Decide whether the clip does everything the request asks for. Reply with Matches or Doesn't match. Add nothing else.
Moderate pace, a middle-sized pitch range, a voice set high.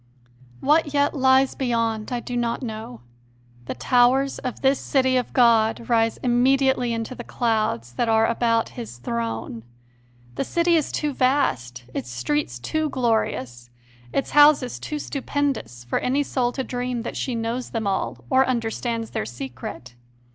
Matches